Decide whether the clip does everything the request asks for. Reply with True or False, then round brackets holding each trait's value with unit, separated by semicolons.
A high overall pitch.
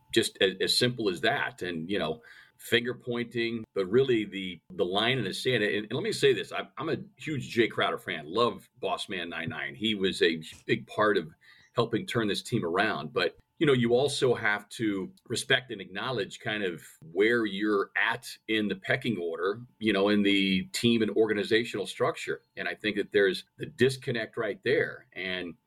False (110 Hz)